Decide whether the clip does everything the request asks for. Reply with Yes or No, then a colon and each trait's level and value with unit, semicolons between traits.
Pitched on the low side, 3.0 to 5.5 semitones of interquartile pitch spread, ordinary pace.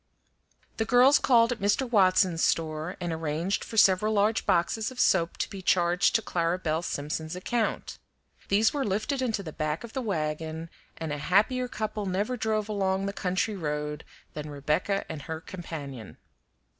No: medium, 185 Hz; average, 5.2 semitones; average, 170 wpm